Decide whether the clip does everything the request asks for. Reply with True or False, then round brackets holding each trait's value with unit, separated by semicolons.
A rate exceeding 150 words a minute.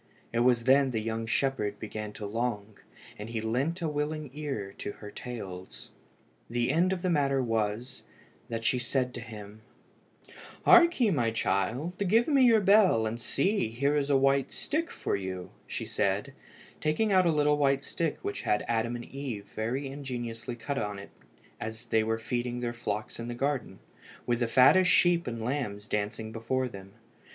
True (180 wpm)